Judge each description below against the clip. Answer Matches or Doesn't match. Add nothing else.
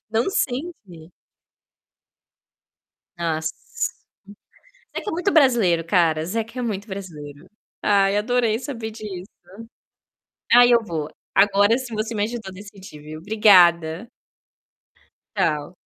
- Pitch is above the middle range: Matches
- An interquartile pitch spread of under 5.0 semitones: Doesn't match